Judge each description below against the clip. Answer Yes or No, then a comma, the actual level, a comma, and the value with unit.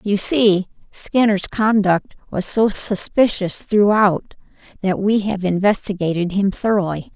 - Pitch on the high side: Yes, high, 195 Hz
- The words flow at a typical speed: No, slow, 115 wpm